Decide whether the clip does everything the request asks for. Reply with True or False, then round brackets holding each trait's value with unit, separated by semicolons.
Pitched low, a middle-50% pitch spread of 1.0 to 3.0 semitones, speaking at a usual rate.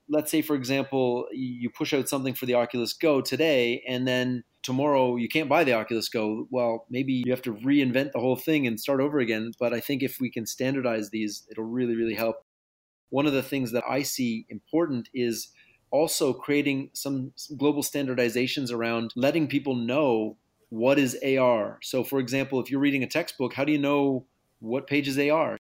True (130 Hz; 2.7 semitones; 195 wpm)